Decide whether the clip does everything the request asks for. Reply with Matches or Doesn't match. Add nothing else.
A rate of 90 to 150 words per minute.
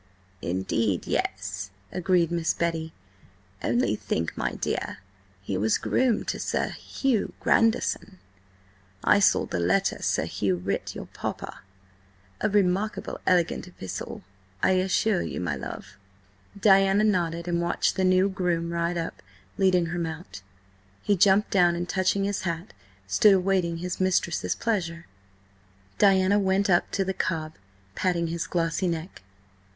Matches